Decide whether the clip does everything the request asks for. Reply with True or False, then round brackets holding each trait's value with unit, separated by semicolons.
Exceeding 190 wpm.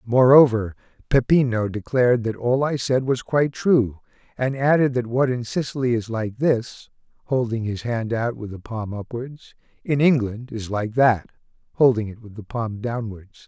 False (170 wpm)